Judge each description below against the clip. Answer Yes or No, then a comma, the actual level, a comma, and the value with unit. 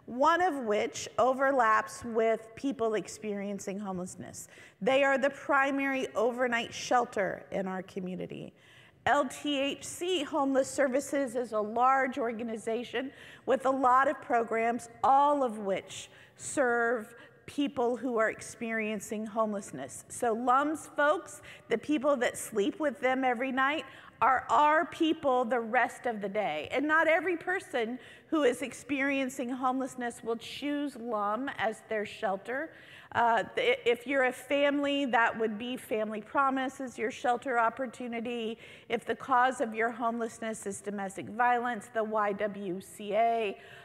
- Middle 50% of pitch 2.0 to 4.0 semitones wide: Yes, average, 3.6 semitones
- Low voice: No, high, 245 Hz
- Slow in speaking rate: Yes, slow, 130 wpm